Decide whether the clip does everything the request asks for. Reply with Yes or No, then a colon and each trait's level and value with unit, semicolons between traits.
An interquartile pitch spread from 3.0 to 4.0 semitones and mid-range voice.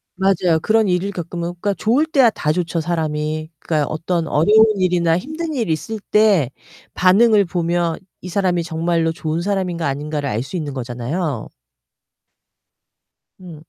Yes: average, 3.7 semitones; medium, 175 Hz